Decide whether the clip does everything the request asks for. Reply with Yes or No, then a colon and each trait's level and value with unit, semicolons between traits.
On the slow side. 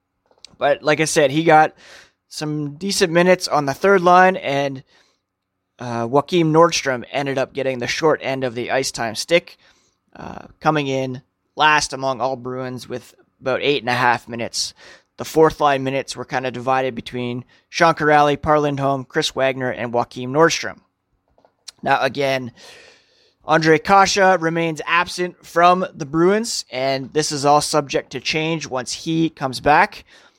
No: average, 155 wpm